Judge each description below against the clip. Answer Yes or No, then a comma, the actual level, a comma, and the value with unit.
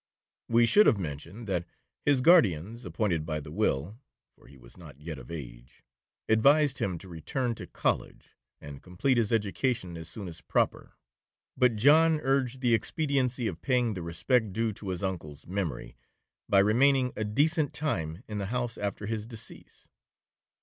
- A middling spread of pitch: No, wide, 6.9 semitones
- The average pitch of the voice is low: Yes, low, 105 Hz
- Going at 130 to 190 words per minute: Yes, average, 165 wpm